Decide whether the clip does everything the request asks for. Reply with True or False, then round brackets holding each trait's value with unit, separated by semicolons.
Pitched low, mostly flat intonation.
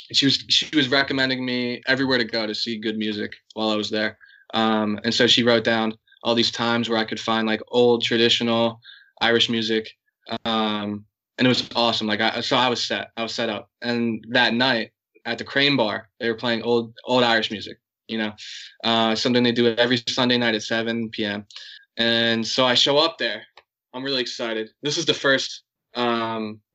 True (115 Hz; 1.7 semitones)